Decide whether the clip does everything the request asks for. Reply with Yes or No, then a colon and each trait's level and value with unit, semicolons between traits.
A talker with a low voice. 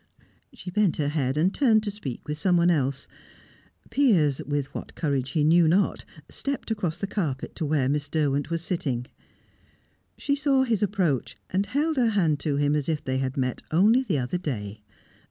No: medium, 160 Hz